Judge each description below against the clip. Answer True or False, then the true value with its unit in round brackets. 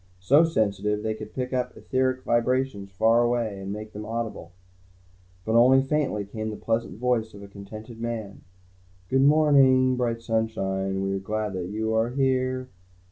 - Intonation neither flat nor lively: True (3.6 semitones)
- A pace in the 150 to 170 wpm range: True (155 wpm)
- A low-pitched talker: True (115 Hz)